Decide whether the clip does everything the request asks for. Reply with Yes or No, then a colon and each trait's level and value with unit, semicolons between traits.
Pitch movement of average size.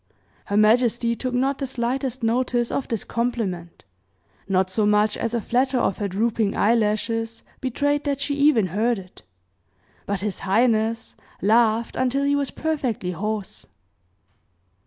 Yes: average, 3.4 semitones